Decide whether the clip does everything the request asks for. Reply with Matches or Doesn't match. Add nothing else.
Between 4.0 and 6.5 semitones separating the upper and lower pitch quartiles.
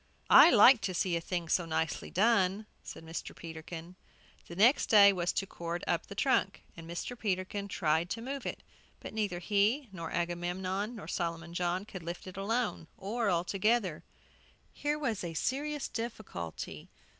Matches